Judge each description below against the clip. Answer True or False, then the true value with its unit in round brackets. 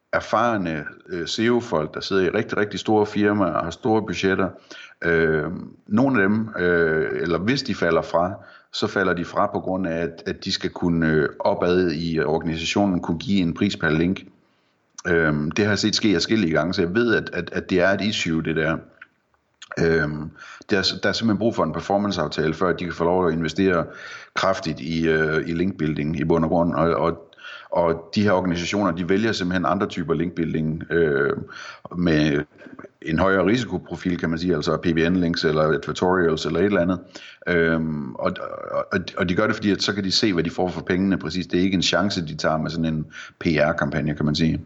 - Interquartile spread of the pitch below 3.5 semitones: True (3.1 semitones)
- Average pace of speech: True (190 wpm)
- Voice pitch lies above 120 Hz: False (85 Hz)